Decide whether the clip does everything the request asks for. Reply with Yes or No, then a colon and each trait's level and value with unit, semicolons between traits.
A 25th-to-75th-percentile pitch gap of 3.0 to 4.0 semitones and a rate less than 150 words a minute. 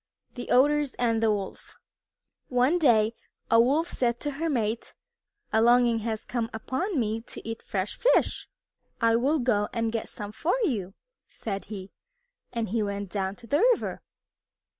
No: average, 3.5 semitones; average, 165 wpm